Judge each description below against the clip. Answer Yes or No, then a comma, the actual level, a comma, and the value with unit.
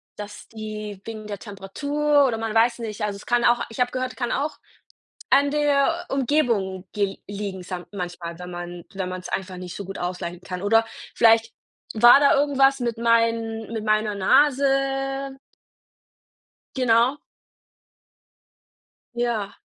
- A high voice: Yes, high, 225 Hz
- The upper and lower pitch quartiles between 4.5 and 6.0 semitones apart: Yes, average, 5.1 semitones